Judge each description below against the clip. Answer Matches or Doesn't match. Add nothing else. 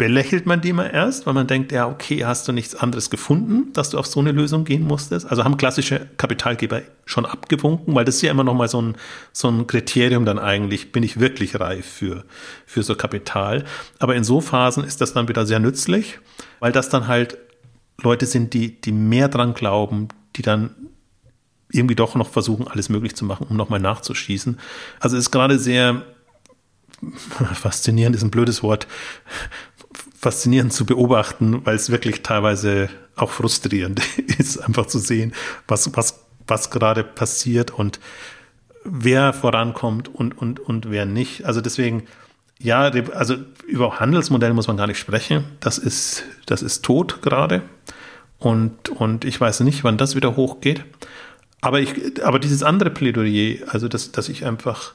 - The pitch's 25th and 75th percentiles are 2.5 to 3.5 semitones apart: Matches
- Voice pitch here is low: Matches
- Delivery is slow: Doesn't match